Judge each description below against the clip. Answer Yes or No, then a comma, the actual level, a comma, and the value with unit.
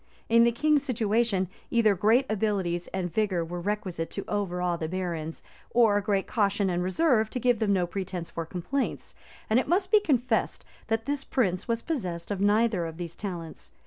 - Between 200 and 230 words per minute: No, average, 180 wpm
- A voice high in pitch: Yes, high, 205 Hz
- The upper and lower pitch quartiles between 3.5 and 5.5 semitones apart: Yes, average, 4.7 semitones